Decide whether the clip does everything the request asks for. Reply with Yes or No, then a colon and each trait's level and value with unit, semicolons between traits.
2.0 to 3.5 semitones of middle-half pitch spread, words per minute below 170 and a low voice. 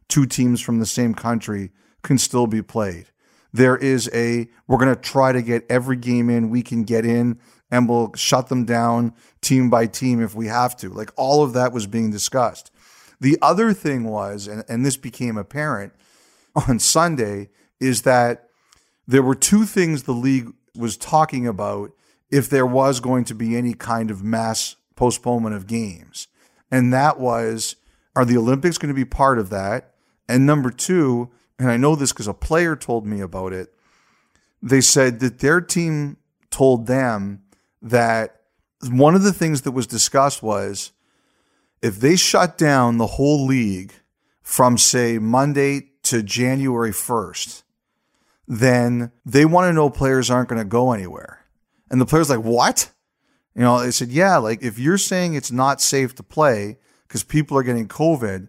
No: average, 3.0 semitones; average, 175 wpm; low, 125 Hz